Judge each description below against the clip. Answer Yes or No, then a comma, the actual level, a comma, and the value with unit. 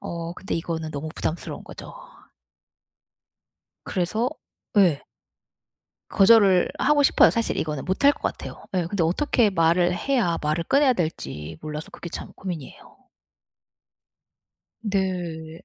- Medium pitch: Yes, medium, 175 Hz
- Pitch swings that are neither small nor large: Yes, average, 4.1 semitones